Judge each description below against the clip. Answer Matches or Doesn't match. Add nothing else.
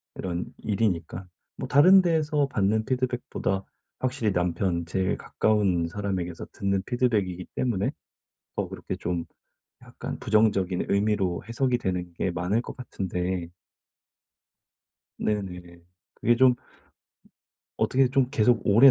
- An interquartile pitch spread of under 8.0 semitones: Matches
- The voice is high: Doesn't match